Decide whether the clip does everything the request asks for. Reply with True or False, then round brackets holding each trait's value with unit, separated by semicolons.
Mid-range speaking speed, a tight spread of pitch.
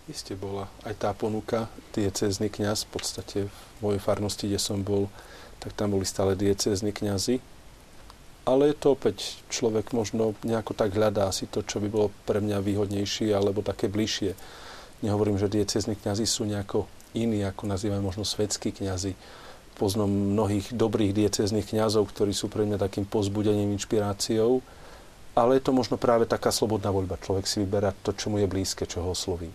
False (170 wpm; 1.6 semitones)